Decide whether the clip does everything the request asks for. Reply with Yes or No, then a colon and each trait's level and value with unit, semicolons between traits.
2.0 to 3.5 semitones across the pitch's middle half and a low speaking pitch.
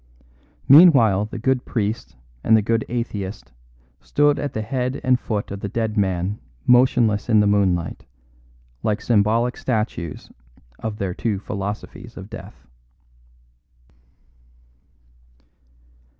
Yes: average, 3.1 semitones; low, 110 Hz